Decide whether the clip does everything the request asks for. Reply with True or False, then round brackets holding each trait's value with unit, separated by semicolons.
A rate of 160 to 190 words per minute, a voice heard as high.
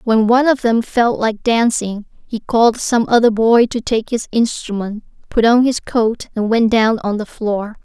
False (200 wpm; 225 Hz)